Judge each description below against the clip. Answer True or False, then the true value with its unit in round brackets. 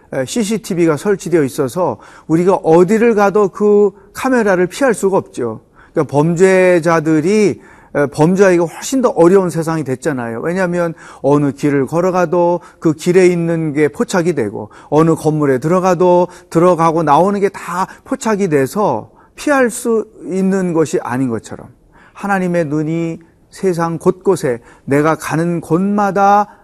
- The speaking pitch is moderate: True (175 Hz)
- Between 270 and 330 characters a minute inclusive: True (305 characters per minute)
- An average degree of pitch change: True (3.5 semitones)